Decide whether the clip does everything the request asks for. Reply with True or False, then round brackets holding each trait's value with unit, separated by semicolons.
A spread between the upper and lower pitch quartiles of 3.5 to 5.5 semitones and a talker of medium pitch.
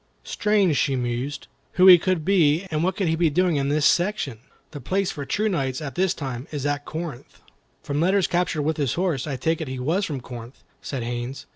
True (4.8 semitones; 150 Hz)